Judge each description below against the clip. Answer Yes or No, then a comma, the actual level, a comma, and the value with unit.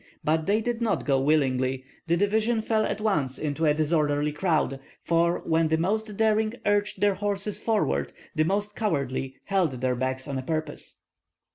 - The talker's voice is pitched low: No, medium, 165 Hz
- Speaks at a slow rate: No, average, 165 wpm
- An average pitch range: No, wide, 6.2 semitones